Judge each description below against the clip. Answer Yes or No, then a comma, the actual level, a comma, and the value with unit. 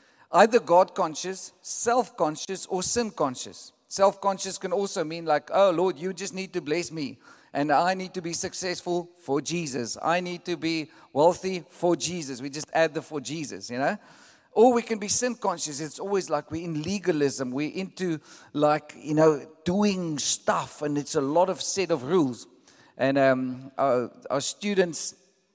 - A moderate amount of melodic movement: Yes, average, 3.9 semitones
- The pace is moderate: Yes, average, 180 wpm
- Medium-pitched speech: Yes, medium, 175 Hz